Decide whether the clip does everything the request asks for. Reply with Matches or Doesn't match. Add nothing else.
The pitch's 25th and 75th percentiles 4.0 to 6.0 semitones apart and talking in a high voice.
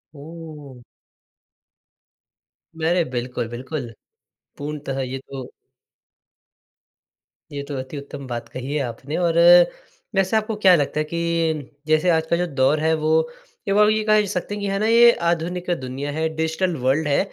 Doesn't match